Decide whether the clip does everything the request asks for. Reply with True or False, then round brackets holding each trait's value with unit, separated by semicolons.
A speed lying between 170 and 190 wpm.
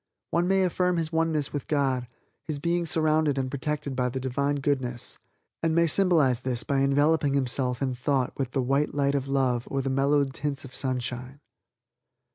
True (180 wpm)